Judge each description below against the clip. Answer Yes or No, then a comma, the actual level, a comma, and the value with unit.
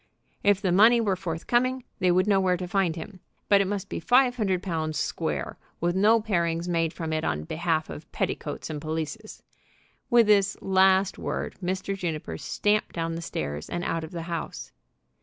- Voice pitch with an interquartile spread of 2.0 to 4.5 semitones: Yes, average, 3.6 semitones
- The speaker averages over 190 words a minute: No, average, 185 wpm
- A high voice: No, medium, 180 Hz